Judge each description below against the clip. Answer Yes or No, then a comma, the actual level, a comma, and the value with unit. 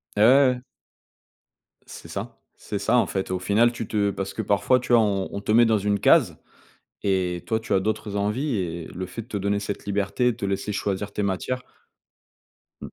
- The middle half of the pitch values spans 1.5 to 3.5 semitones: Yes, narrow, 2.6 semitones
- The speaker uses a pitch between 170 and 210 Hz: No, low, 100 Hz